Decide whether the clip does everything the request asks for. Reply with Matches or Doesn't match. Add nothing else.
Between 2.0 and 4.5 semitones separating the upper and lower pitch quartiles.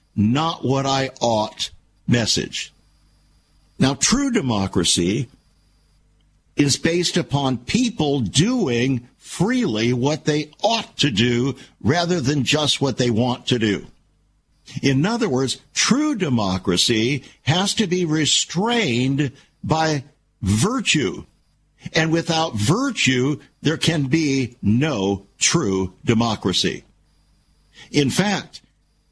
Doesn't match